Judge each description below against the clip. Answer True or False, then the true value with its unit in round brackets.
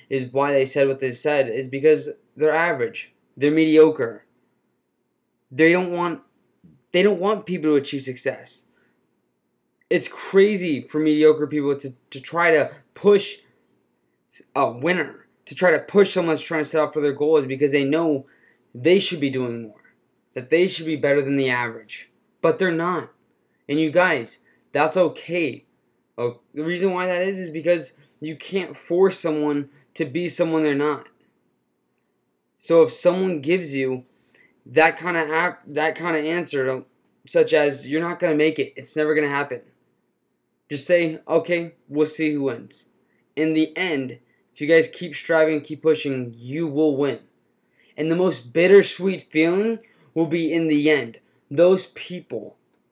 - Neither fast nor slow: True (165 wpm)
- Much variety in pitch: False (3.6 semitones)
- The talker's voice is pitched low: False (155 Hz)